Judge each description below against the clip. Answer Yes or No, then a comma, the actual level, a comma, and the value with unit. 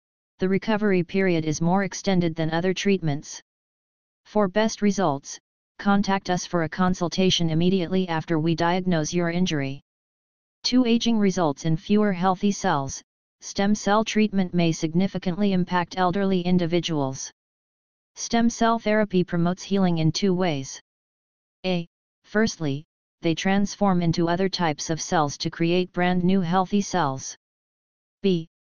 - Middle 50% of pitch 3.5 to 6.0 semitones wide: No, average, 2.9 semitones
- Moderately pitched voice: Yes, medium, 180 Hz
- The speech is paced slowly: Yes, slow, 130 wpm